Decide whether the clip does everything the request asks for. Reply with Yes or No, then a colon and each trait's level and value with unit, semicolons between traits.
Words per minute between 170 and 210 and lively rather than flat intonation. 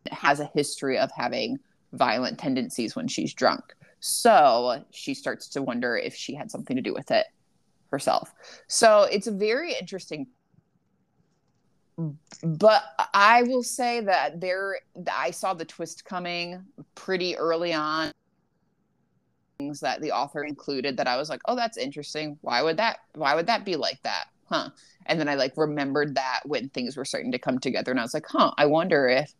Yes: average, 175 wpm; wide, 6.0 semitones